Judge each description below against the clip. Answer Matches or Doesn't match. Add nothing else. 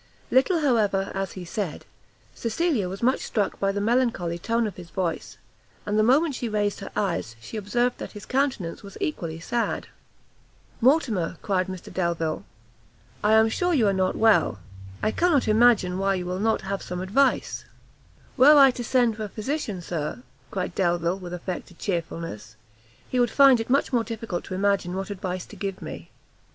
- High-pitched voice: Matches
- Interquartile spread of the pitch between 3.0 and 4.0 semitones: Doesn't match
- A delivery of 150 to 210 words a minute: Matches